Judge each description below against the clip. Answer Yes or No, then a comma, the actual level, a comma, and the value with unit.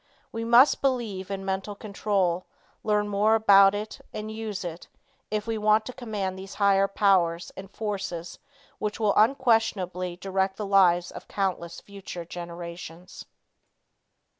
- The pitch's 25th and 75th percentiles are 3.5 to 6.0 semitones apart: No, average, 2.7 semitones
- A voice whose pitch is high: Yes, high, 195 Hz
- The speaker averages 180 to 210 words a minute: No, average, 140 wpm